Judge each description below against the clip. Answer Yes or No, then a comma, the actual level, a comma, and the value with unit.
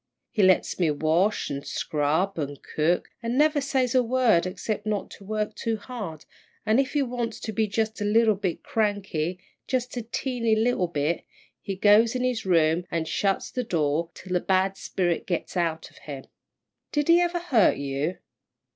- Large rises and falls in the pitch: Yes, wide, 5.7 semitones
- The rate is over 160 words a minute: Yes, average, 180 wpm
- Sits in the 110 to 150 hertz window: No, high, 205 Hz